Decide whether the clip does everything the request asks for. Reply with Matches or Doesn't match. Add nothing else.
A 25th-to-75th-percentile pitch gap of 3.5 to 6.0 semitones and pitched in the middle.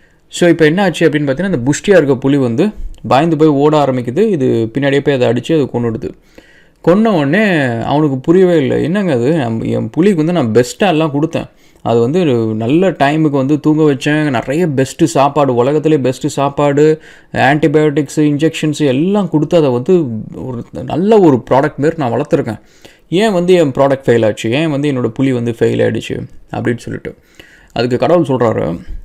Matches